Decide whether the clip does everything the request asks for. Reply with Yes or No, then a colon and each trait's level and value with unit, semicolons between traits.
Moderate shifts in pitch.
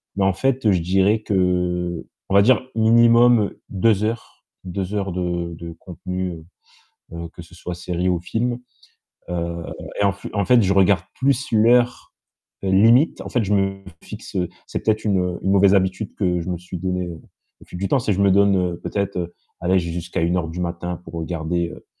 Yes: average, 3.0 semitones